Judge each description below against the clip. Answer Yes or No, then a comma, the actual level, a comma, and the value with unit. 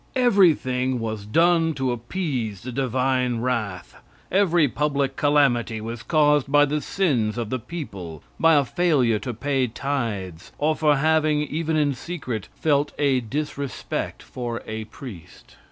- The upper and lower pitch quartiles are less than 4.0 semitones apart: No, average, 4.5 semitones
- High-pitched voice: No, low, 135 Hz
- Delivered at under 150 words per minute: Yes, average, 140 wpm